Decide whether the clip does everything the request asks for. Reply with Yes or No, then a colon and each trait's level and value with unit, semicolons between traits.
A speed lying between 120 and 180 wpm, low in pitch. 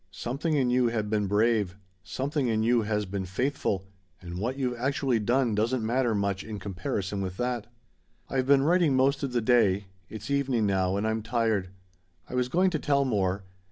No: average, 190 wpm; low, 115 Hz